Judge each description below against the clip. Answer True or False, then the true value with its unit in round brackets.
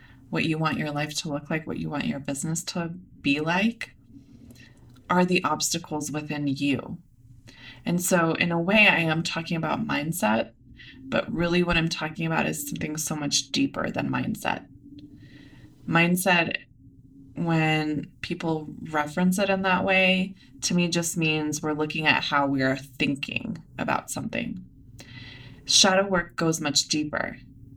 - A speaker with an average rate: True (150 wpm)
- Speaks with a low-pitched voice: False (155 Hz)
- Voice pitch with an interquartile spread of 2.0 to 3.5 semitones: False (3.9 semitones)